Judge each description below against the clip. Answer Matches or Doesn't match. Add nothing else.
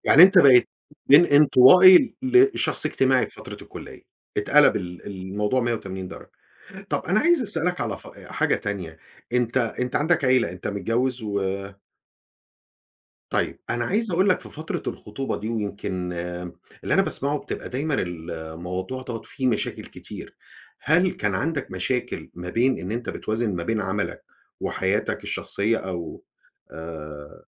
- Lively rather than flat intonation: Matches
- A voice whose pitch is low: Matches